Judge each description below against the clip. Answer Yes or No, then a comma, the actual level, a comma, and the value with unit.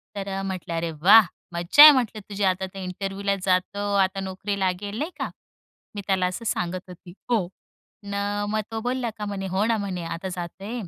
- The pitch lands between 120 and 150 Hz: No, high, 195 Hz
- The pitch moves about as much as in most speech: No, narrow, 2.1 semitones